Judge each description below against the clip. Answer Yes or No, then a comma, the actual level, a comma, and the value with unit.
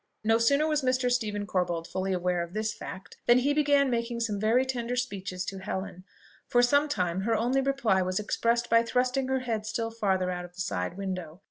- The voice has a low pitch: No, high, 225 Hz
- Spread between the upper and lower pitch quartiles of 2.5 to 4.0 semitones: No, average, 5.0 semitones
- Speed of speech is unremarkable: No, fast, 210 wpm